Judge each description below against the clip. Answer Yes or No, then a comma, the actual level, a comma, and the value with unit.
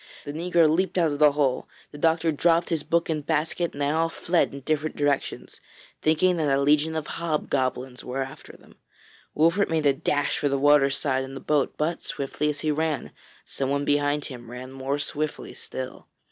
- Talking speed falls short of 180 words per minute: No, average, 195 wpm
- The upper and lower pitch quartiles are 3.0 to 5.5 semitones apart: No, narrow, 2.5 semitones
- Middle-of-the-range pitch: Yes, medium, 150 Hz